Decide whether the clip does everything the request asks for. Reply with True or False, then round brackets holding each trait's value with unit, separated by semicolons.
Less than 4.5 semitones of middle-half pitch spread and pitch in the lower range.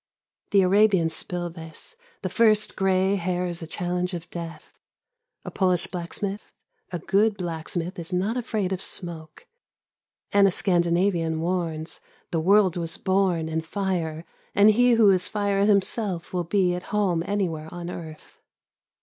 False (2.9 semitones; 180 Hz)